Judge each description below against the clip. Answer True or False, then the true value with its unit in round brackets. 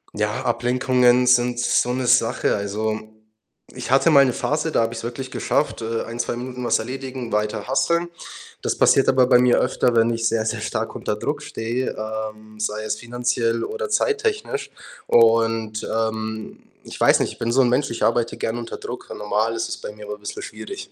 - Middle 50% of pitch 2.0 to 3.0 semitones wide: True (2.4 semitones)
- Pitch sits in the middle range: False (120 Hz)